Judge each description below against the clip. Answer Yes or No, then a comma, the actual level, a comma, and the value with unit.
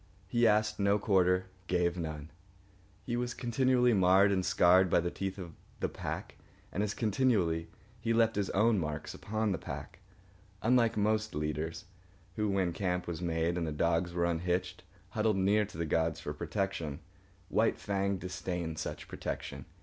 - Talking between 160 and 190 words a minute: Yes, average, 165 wpm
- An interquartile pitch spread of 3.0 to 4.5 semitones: Yes, average, 3.9 semitones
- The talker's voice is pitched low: Yes, very low, 95 Hz